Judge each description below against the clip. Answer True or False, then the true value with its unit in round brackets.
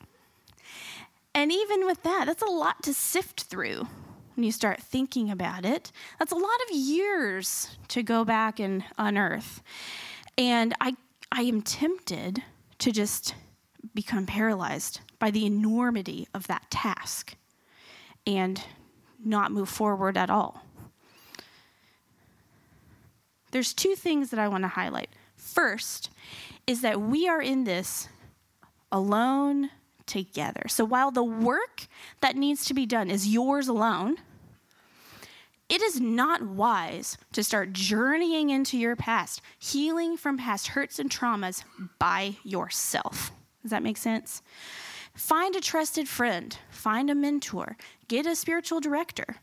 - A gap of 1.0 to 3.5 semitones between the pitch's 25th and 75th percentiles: False (5.5 semitones)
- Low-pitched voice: False (245 Hz)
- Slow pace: True (130 wpm)